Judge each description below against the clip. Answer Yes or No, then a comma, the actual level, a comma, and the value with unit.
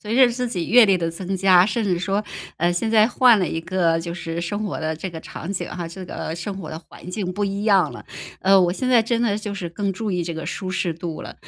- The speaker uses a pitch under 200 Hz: Yes, high, 190 Hz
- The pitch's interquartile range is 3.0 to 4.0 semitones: Yes, average, 3.5 semitones